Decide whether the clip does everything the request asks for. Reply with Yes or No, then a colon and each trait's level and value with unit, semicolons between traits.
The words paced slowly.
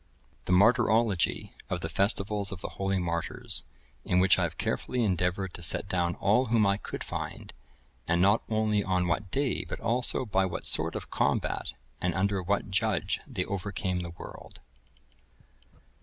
No: average, 165 wpm